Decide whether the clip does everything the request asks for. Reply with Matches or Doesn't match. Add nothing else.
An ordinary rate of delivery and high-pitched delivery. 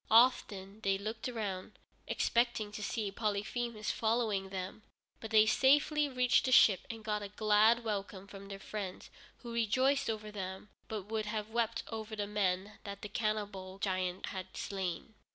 Matches